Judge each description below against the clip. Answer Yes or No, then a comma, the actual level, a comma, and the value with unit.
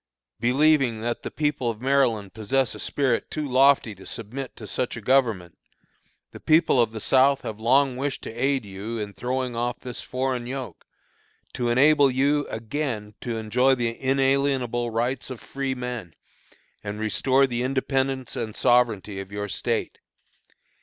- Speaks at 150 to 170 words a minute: Yes, average, 155 wpm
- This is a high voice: No, low, 125 Hz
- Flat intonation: No, average, 3.1 semitones